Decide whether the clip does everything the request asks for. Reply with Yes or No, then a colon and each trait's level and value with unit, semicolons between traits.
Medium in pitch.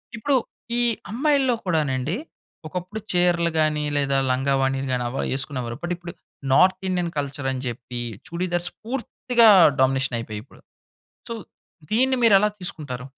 Yes: medium, 170 Hz